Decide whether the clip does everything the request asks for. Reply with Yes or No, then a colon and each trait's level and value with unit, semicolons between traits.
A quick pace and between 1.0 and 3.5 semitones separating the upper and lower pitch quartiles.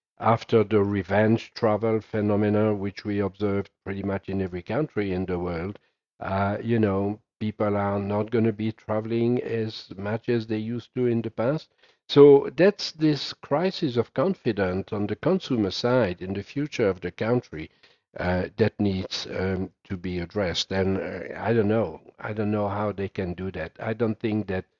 No: average, 180 wpm; average, 2.9 semitones